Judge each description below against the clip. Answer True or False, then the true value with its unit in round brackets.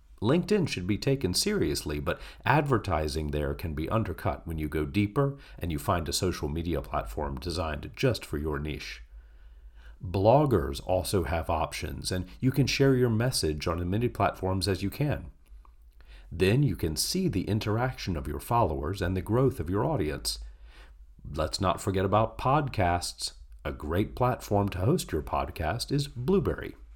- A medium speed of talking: True (165 wpm)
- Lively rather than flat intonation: True (7.9 semitones)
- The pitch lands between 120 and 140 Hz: False (90 Hz)